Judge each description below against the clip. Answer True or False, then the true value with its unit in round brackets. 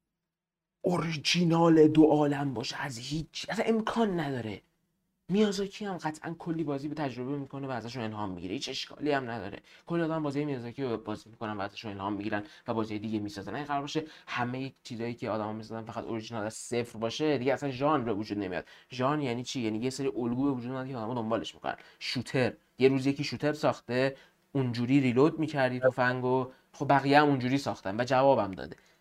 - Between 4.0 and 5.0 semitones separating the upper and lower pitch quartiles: True (4.7 semitones)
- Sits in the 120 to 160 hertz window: True (135 Hz)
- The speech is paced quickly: True (185 wpm)